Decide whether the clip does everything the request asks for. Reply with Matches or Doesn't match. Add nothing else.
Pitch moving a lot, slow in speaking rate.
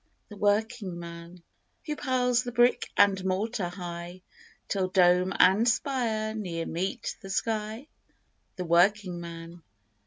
Doesn't match